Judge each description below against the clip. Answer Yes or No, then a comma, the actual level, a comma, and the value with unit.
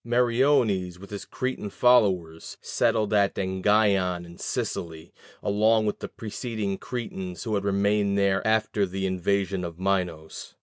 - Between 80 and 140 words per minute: Yes, slow, 135 wpm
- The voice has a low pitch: Yes, low, 100 Hz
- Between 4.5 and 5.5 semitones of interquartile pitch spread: No, average, 2.8 semitones